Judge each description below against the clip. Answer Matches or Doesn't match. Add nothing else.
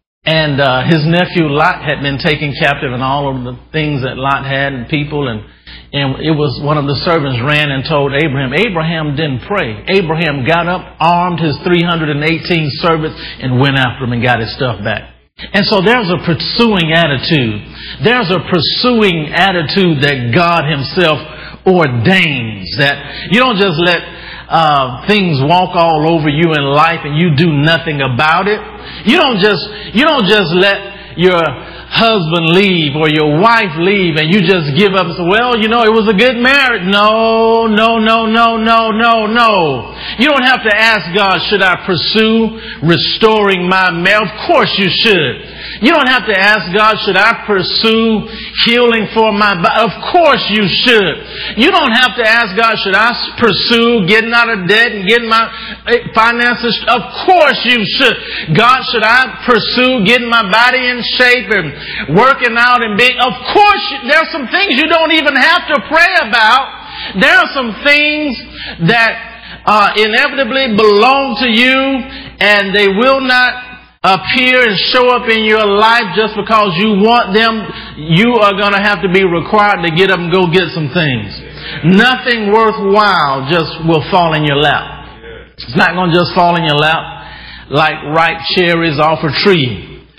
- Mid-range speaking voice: Doesn't match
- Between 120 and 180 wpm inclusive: Matches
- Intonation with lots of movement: Matches